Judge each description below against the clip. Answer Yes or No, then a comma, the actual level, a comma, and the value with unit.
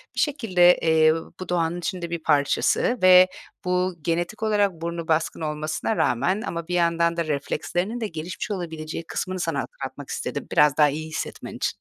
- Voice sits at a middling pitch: Yes, medium, 170 Hz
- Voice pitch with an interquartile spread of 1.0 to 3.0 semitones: Yes, narrow, 2.6 semitones